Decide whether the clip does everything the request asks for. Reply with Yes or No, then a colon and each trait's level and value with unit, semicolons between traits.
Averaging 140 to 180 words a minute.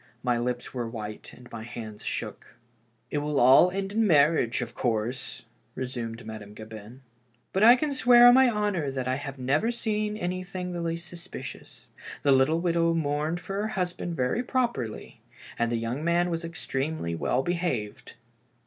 Yes: average, 175 wpm